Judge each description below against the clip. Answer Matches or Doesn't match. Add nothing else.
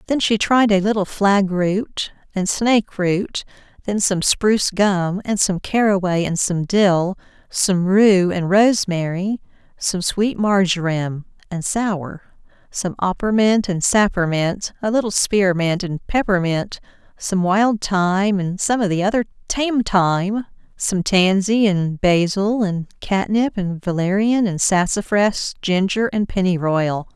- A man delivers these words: Doesn't match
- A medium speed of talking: Doesn't match